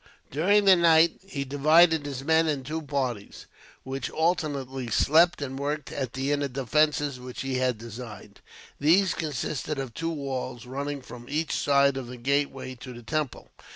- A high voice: No, medium, 140 Hz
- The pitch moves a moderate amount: Yes, average, 3.2 semitones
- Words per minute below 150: No, average, 165 wpm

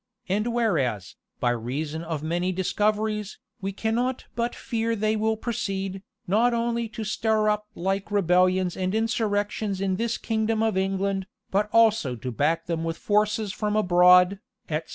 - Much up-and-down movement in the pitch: No, average, 3.6 semitones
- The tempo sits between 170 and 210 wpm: No, average, 155 wpm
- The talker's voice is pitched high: Yes, high, 200 Hz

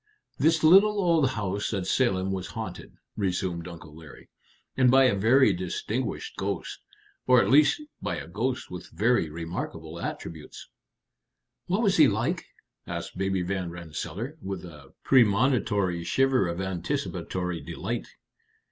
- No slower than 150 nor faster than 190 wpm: No, slow, 135 wpm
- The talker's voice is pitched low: Yes, very low, 95 Hz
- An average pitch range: No, wide, 7.0 semitones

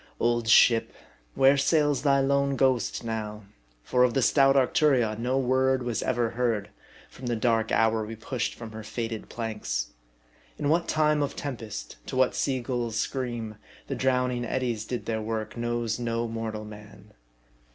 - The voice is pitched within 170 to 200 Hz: No, low, 120 Hz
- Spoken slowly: No, average, 160 wpm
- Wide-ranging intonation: No, average, 2.8 semitones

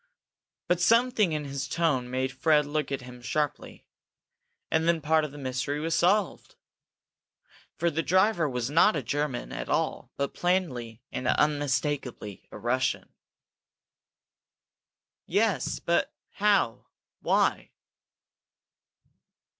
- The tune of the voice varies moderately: Yes, average, 4.7 semitones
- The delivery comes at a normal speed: No, slow, 115 wpm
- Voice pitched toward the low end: No, medium, 150 Hz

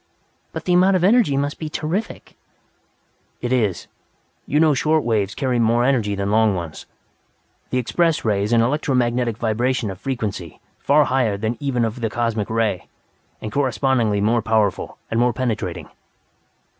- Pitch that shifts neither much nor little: Yes, average, 4.1 semitones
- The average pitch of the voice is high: No, low, 120 Hz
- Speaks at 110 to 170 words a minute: Yes, average, 165 wpm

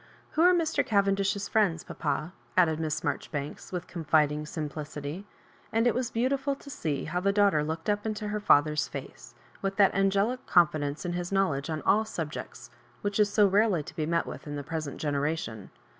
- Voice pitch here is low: No, medium, 175 Hz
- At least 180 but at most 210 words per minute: Yes, average, 190 wpm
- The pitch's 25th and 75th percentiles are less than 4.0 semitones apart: No, average, 5.2 semitones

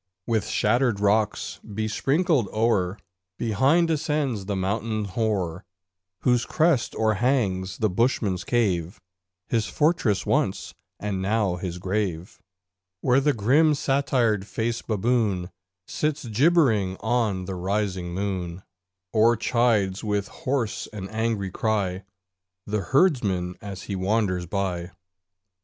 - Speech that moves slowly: Yes, slow, 110 wpm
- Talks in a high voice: No, low, 105 Hz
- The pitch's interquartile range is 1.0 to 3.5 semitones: No, average, 4.0 semitones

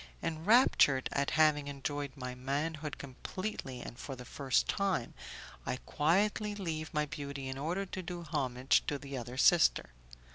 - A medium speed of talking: Yes, average, 150 wpm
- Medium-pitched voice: Yes, medium, 145 Hz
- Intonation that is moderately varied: Yes, average, 3.9 semitones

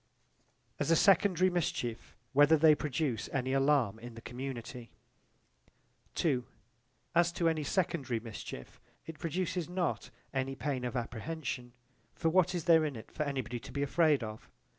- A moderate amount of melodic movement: Yes, average, 5.0 semitones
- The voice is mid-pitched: Yes, medium, 145 Hz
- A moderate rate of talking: Yes, average, 150 wpm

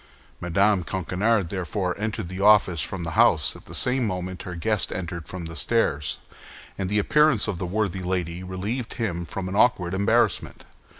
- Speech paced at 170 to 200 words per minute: Yes, average, 175 wpm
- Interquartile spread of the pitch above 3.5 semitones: No, average, 3.1 semitones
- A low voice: Yes, very low, 95 Hz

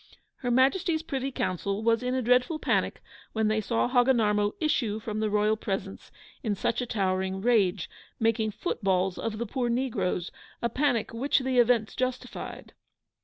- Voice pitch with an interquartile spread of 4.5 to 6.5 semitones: No, average, 3.5 semitones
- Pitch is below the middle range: No, high, 230 Hz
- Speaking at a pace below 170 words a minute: Yes, average, 160 wpm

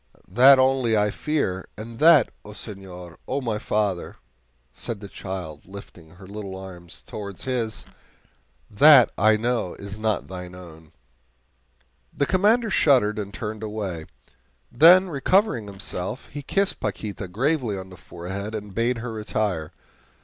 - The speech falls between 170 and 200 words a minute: No, average, 140 wpm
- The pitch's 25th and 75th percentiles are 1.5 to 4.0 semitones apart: No, average, 4.9 semitones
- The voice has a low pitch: Yes, low, 105 Hz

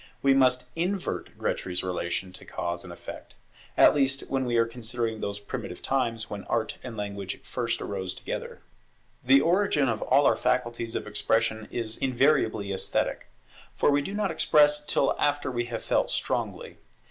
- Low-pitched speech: Yes, low, 120 Hz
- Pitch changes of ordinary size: Yes, average, 4.5 semitones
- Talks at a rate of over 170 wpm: No, average, 165 wpm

